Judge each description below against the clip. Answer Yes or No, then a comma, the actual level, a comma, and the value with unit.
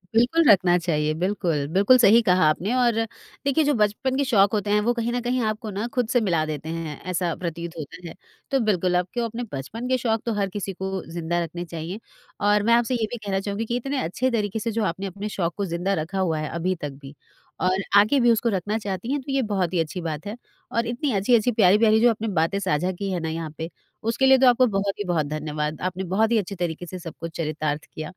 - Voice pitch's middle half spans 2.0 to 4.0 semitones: No, average, 5.2 semitones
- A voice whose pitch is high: Yes, high, 195 Hz